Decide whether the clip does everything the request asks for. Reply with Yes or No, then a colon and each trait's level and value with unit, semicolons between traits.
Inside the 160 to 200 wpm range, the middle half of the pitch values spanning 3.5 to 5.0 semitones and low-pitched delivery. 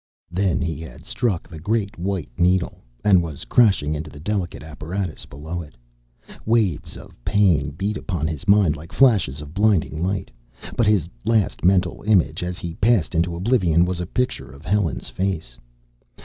Yes: average, 165 wpm; average, 4.3 semitones; very low, 90 Hz